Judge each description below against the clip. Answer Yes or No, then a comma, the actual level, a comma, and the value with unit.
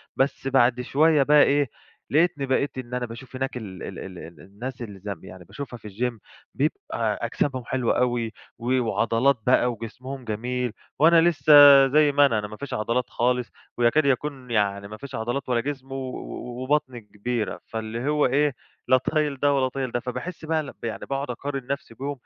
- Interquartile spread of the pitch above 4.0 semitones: No, average, 3.1 semitones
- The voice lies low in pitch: Yes, low, 125 Hz